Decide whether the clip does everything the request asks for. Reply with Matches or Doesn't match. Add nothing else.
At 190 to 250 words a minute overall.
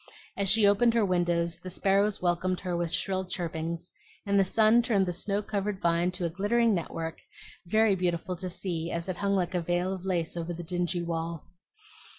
Matches